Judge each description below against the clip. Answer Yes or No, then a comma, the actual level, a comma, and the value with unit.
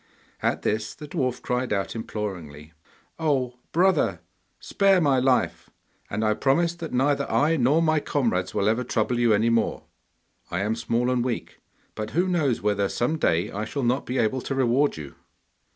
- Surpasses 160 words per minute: Yes, average, 175 wpm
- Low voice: Yes, low, 125 Hz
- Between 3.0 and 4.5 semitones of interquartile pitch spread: No, average, 4.9 semitones